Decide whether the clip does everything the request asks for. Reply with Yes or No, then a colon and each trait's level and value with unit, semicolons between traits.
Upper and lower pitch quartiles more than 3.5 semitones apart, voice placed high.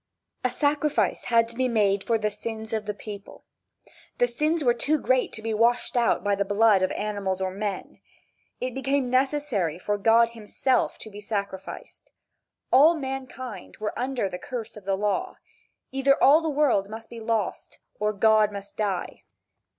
Yes: average, 4.0 semitones; high, 225 Hz